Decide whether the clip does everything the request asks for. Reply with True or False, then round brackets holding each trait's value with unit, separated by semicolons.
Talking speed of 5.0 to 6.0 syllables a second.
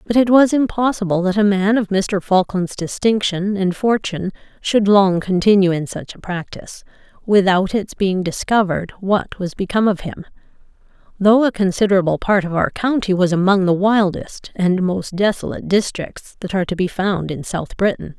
True (5.1 syllables/s)